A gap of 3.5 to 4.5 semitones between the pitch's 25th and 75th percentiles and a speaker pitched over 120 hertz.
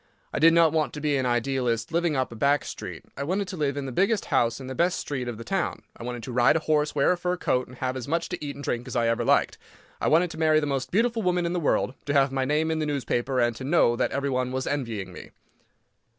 Yes: average, 4.2 semitones; medium, 140 Hz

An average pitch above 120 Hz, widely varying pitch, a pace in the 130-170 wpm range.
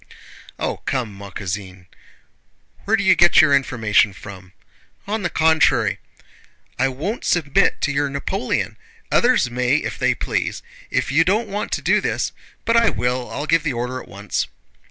Yes: medium, 140 Hz; wide, 7.2 semitones; average, 165 wpm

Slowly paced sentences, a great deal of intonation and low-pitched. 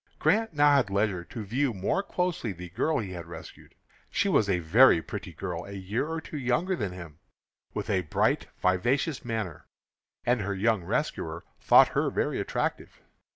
No: average, 175 wpm; wide, 7.0 semitones; low, 105 Hz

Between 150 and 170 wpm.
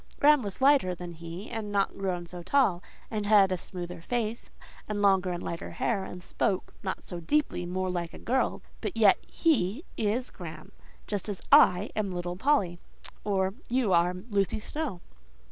Yes: average, 165 wpm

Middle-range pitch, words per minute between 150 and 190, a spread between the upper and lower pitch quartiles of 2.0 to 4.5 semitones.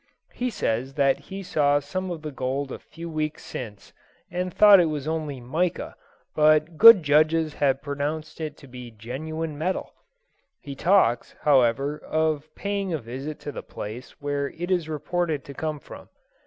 Yes: medium, 150 Hz; average, 170 wpm; average, 2.9 semitones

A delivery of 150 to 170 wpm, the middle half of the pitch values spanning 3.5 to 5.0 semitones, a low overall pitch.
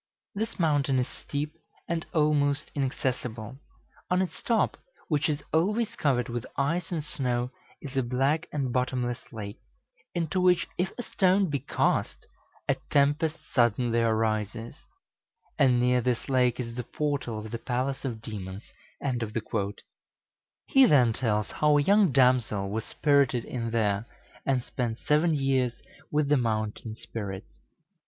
No: average, 140 wpm; average, 4.3 semitones; low, 130 Hz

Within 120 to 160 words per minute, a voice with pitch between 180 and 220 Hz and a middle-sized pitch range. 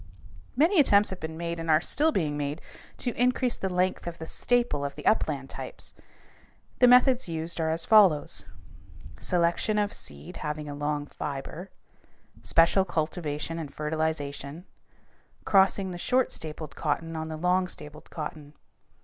No: average, 150 wpm; medium, 165 Hz; average, 4.2 semitones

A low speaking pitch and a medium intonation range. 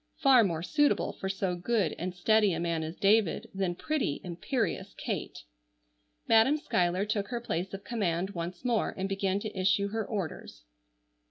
No: high, 195 Hz; average, 4.0 semitones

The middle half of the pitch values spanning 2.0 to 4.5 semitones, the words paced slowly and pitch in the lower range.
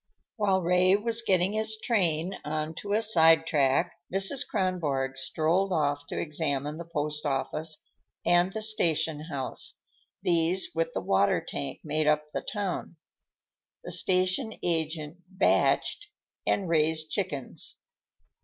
No: average, 4.0 semitones; slow, 125 wpm; medium, 170 Hz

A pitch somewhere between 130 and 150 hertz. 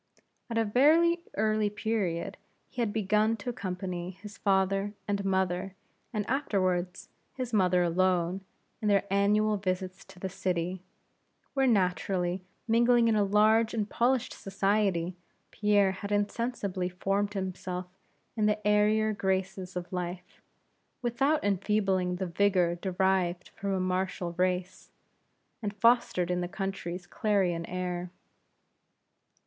No: high, 195 Hz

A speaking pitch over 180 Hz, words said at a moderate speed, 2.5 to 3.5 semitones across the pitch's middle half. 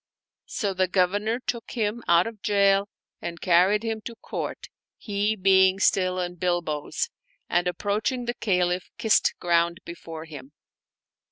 Yes: high, 190 Hz; average, 150 wpm; average, 3.2 semitones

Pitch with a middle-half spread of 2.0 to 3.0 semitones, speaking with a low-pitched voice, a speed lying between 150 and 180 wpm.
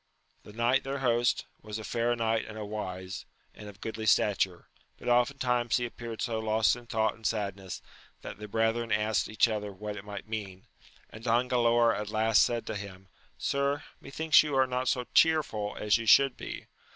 No: narrow, 2.5 semitones; low, 110 Hz; average, 190 wpm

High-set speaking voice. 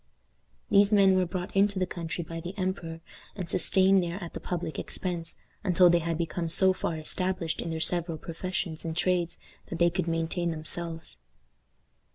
No: medium, 175 Hz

